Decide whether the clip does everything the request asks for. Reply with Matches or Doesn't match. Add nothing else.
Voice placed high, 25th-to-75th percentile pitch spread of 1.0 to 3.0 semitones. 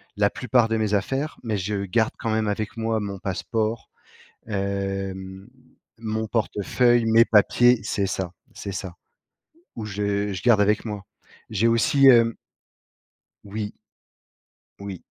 Doesn't match